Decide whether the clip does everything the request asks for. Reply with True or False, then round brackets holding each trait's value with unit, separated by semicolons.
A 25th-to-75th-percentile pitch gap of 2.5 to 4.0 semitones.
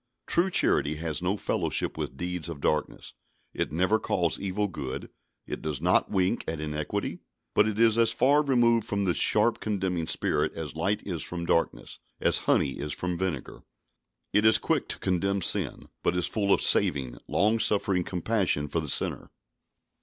False (4.8 semitones)